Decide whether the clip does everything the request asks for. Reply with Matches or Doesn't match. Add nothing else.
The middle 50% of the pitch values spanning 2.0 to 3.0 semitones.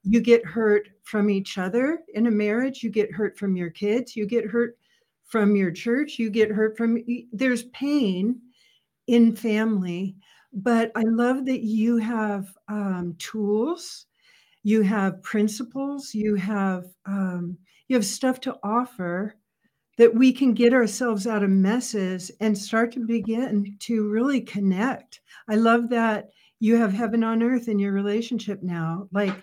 Matches